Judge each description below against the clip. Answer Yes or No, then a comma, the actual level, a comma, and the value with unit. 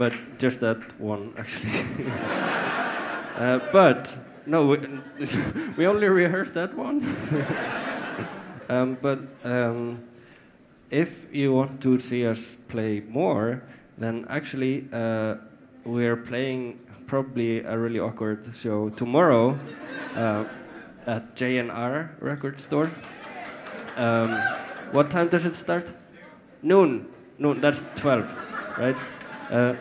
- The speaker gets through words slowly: Yes, slow, 110 wpm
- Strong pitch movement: No, average, 3.6 semitones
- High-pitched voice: No, low, 125 Hz